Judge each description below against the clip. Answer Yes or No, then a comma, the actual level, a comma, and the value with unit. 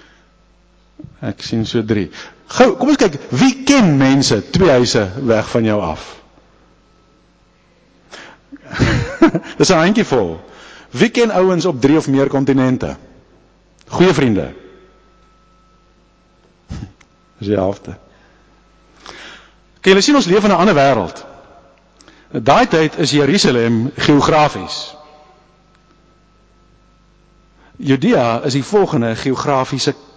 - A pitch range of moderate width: No, wide, 5.7 semitones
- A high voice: No, medium, 140 Hz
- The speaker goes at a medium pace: No, slow, 105 wpm